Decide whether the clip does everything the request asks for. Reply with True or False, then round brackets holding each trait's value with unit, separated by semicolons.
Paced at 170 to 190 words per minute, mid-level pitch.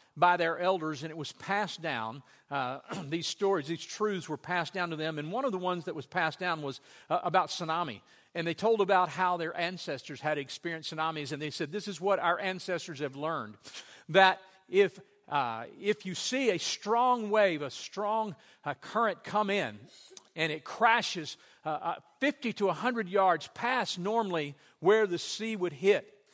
True (185 wpm; 180 Hz)